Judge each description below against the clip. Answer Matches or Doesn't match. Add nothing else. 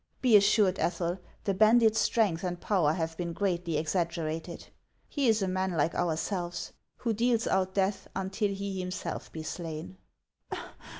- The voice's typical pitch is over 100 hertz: Matches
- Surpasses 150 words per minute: Doesn't match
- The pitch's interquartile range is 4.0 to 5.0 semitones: Doesn't match